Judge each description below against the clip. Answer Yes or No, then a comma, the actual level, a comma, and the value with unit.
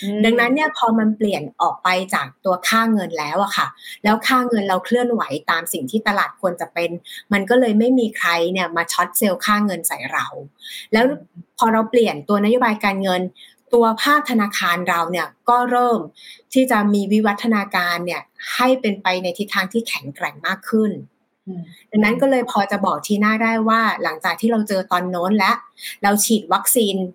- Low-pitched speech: No, high, 210 Hz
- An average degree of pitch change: Yes, average, 4.0 semitones